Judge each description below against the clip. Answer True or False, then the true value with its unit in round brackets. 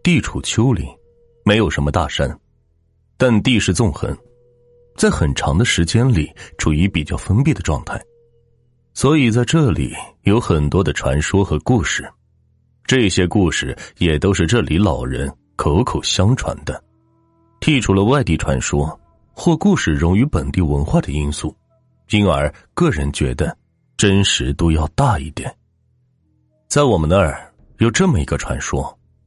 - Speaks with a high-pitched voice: False (100 Hz)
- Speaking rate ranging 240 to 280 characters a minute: False (215 characters per minute)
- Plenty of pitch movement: True (7.5 semitones)